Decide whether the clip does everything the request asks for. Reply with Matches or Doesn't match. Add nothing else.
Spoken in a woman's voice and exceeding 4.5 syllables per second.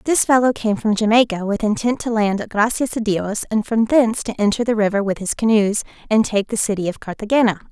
Matches